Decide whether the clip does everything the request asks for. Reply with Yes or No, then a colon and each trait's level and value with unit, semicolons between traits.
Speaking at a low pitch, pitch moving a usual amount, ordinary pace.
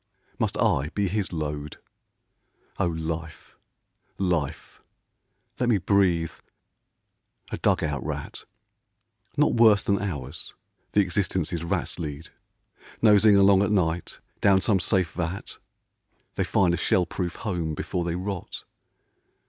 No: very low, 90 Hz; average, 3.5 semitones; slow, 130 wpm